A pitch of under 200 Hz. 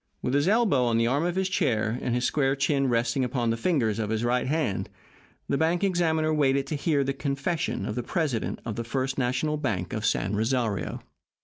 Yes: low, 135 Hz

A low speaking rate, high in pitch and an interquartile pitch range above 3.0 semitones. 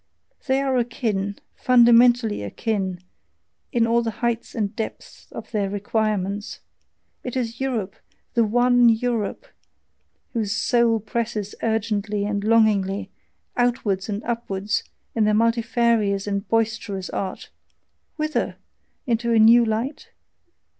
No: slow, 115 wpm; high, 225 Hz; narrow, 2.6 semitones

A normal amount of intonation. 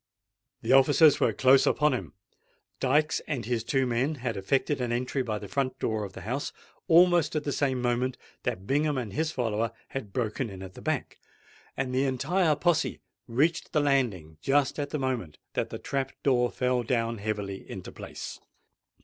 Yes: average, 3.7 semitones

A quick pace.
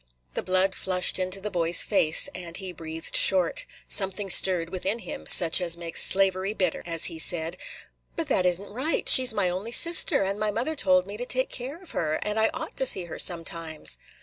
Yes: fast, 210 wpm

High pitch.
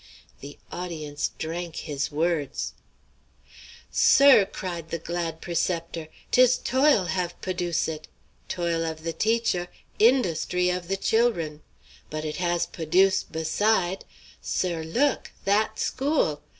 No: medium, 175 Hz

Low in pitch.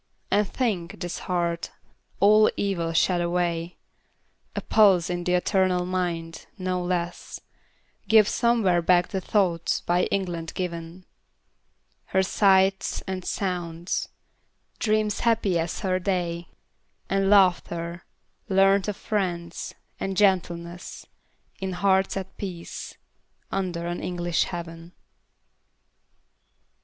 No: medium, 180 Hz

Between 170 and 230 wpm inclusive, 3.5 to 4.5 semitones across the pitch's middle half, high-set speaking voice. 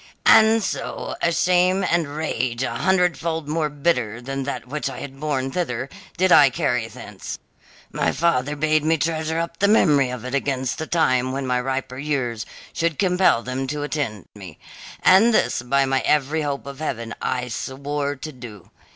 No: average, 175 wpm; average, 4.1 semitones; medium, 140 Hz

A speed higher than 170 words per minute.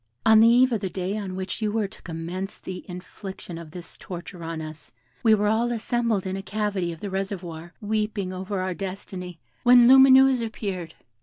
Yes: average, 190 wpm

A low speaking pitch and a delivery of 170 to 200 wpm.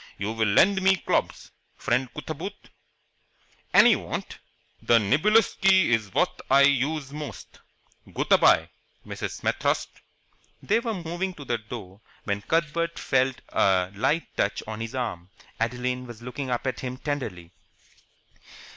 No: low, 130 Hz; average, 145 wpm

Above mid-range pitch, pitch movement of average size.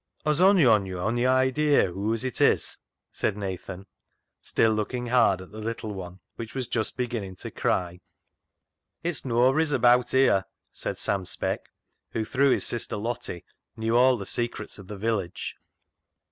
No: low, 115 Hz; average, 4.4 semitones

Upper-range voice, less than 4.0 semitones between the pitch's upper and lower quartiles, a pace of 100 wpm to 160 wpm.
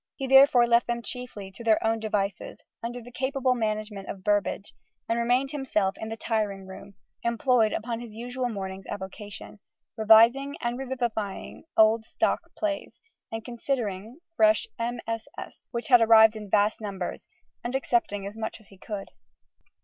Yes: high, 225 Hz; average, 2.8 semitones; average, 150 wpm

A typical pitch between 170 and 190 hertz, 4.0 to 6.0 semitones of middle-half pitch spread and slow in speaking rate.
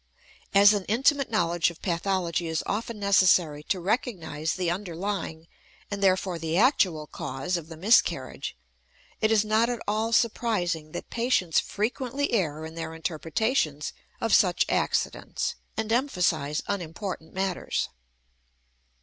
Yes: medium, 185 Hz; average, 5.0 semitones; slow, 130 wpm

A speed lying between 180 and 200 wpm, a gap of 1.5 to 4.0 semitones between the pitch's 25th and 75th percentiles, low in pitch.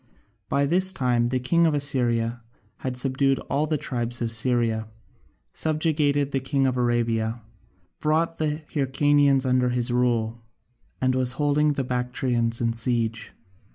No: average, 140 wpm; average, 3.3 semitones; low, 130 Hz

